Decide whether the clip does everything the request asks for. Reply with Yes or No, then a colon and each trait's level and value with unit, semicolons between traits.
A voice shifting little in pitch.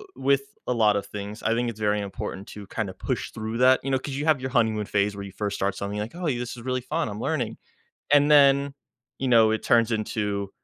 No: average, 4.2 semitones